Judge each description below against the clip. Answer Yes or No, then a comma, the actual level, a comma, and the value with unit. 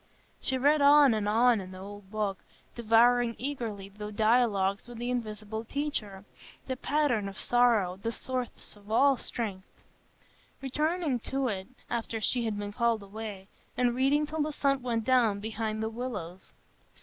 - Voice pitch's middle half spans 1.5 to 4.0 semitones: Yes, average, 3.7 semitones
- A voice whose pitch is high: Yes, high, 230 Hz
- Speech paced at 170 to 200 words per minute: No, average, 160 wpm